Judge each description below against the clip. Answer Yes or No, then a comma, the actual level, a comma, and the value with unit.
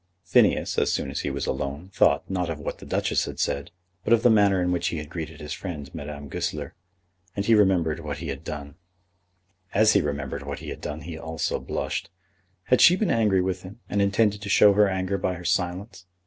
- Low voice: Yes, very low, 90 Hz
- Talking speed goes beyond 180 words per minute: Yes, average, 195 wpm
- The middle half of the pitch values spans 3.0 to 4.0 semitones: No, average, 4.7 semitones